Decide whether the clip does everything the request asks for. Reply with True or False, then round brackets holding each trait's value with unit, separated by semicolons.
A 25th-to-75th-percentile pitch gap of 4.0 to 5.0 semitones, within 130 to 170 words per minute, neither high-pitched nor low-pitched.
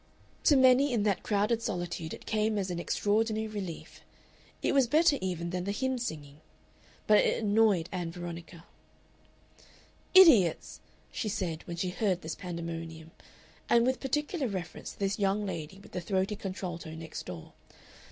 False (4.5 semitones; 155 wpm; 195 Hz)